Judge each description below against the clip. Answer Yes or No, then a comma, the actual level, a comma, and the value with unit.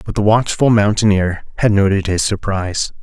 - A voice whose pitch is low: Yes, low, 100 Hz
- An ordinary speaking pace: Yes, average, 160 wpm